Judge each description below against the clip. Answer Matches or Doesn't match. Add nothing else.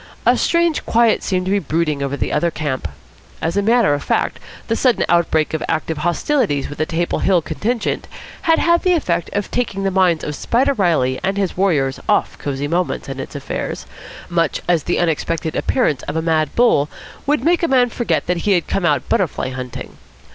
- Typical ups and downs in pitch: Doesn't match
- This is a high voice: Doesn't match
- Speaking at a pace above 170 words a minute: Matches